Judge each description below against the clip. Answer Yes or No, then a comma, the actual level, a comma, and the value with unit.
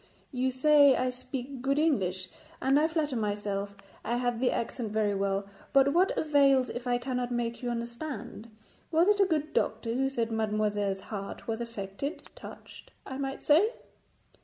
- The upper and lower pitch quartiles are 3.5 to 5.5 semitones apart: Yes, average, 4.3 semitones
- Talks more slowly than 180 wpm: Yes, average, 165 wpm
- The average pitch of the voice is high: Yes, very high, 250 Hz